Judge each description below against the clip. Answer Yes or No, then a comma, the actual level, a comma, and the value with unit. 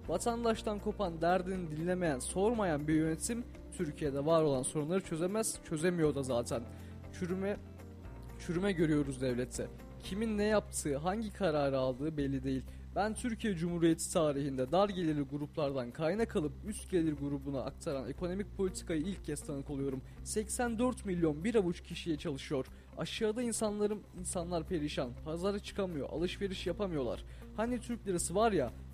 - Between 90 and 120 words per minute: No, average, 135 wpm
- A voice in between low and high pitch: Yes, medium, 170 Hz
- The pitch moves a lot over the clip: Yes, wide, 6.1 semitones